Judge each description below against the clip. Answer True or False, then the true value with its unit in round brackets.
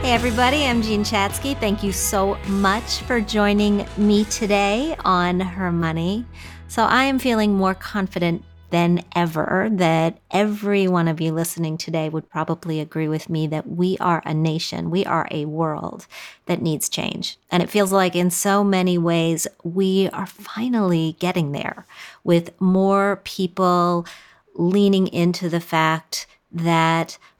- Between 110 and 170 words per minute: True (150 wpm)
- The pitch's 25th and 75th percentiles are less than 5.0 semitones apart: True (3.5 semitones)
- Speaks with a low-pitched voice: False (180 Hz)